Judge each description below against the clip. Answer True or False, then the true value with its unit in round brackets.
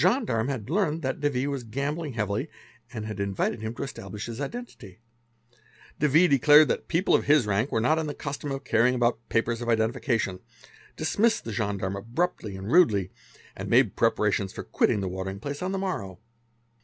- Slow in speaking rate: False (190 wpm)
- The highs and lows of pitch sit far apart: True (6.0 semitones)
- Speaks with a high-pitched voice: False (120 Hz)